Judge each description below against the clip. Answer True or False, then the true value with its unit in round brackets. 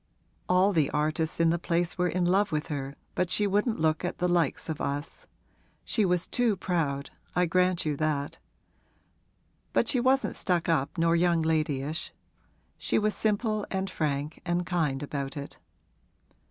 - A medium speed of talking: True (165 wpm)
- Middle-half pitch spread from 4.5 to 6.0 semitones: False (3.3 semitones)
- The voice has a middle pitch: True (170 Hz)